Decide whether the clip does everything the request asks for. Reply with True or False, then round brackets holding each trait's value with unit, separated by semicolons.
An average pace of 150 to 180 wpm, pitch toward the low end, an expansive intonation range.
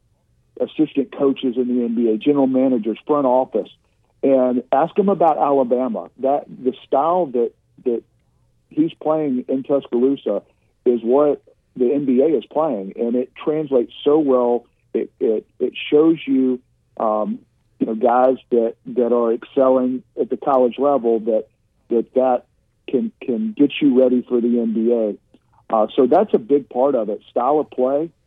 False (155 wpm; 130 Hz; 3.1 semitones)